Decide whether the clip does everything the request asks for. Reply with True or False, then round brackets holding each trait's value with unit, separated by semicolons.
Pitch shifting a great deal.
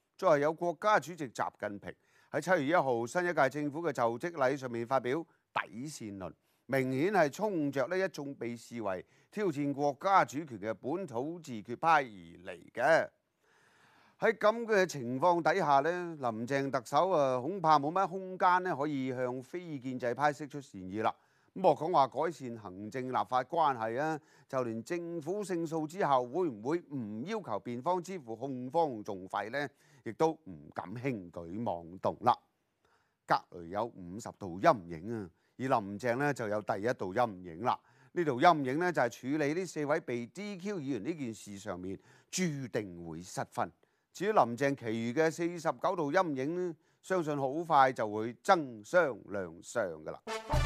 True (6.4 semitones)